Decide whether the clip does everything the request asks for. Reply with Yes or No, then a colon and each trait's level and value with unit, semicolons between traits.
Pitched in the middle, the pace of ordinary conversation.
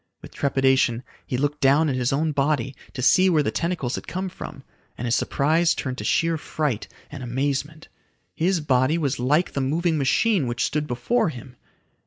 Yes: medium, 145 Hz; average, 185 wpm